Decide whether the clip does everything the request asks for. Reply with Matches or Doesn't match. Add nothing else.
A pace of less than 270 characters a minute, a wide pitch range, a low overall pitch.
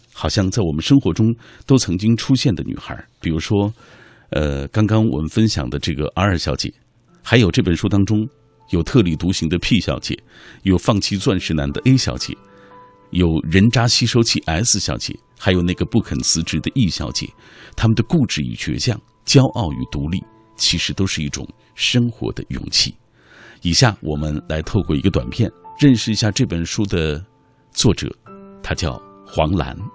Matches